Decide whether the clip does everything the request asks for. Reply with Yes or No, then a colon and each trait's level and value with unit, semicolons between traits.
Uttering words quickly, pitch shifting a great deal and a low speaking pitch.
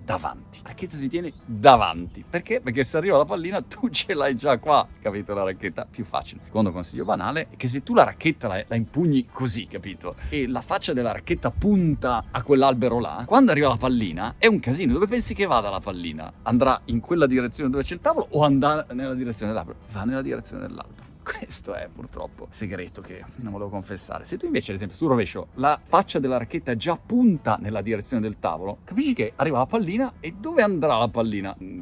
Yes: fast, 210 wpm; wide, 7.7 semitones; low, 125 Hz